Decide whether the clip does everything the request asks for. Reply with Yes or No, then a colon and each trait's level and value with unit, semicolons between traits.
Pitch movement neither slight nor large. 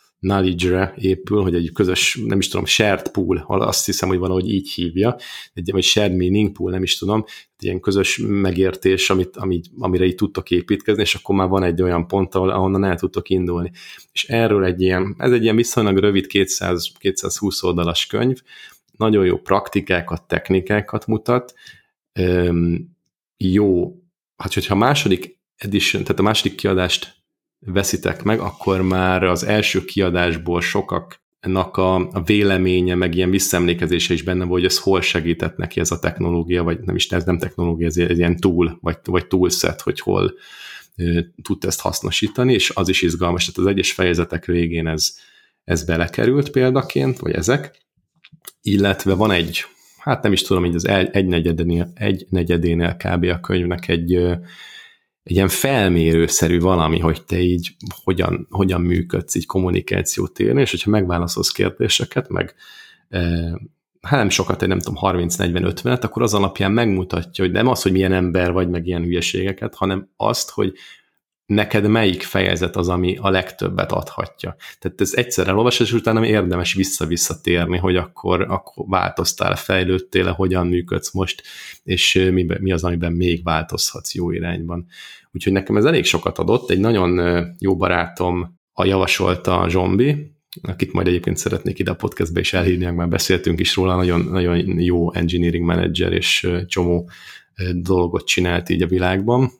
No: narrow, 1.8 semitones